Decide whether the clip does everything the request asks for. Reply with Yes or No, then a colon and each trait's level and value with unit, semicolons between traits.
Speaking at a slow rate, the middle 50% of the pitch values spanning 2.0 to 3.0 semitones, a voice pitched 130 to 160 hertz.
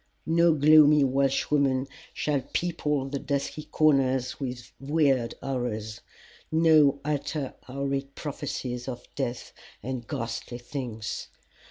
Yes: slow, 105 wpm; average, 2.7 semitones; low, 135 Hz